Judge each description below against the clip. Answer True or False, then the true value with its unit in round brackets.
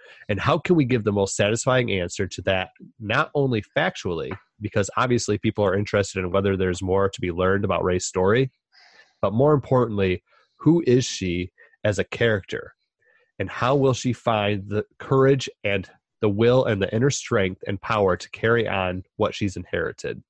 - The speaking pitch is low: True (105 Hz)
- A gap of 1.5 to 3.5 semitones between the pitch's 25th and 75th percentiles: False (4.9 semitones)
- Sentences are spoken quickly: False (175 wpm)